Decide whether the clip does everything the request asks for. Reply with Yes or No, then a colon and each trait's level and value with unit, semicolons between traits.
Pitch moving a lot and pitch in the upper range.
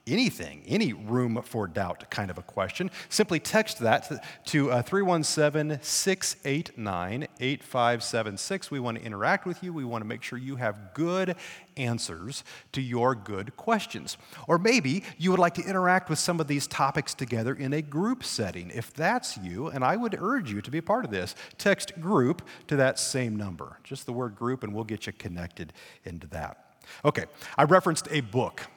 No: wide, 6.8 semitones; low, 135 Hz